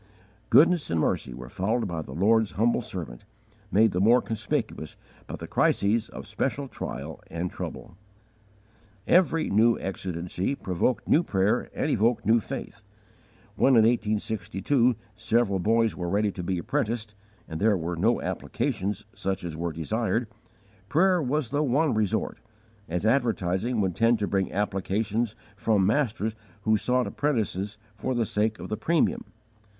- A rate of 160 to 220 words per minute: No, average, 145 wpm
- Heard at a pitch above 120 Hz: No, low, 110 Hz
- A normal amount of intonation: Yes, average, 4.1 semitones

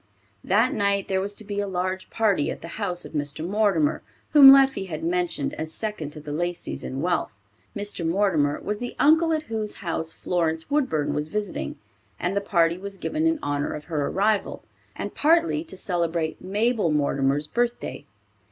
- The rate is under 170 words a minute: No, average, 180 wpm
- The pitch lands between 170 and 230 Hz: Yes, medium, 185 Hz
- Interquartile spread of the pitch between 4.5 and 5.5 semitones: Yes, average, 5.0 semitones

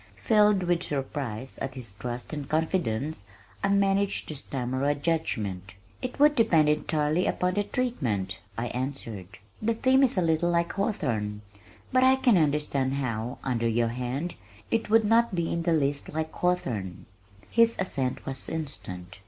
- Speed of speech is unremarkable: Yes, average, 160 wpm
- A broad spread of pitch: Yes, wide, 7.5 semitones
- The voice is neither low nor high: Yes, medium, 150 Hz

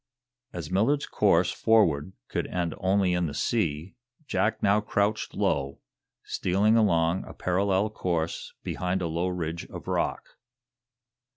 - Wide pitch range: No, average, 3.5 semitones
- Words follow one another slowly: Yes, slow, 130 wpm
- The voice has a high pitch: No, very low, 90 Hz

